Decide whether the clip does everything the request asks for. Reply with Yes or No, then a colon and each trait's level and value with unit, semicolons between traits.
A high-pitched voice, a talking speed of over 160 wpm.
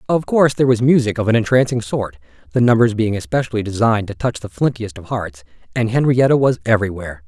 No: low, 115 Hz; average, 200 wpm